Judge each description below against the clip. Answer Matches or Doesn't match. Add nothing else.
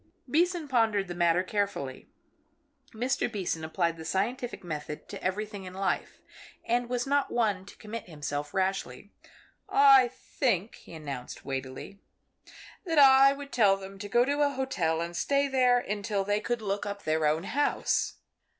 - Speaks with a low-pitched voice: Doesn't match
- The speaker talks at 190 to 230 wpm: Doesn't match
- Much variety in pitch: Matches